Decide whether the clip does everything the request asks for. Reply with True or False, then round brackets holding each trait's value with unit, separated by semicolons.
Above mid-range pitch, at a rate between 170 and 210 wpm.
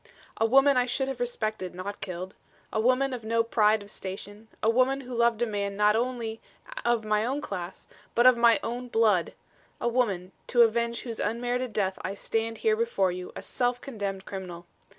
True (225 Hz; 190 wpm)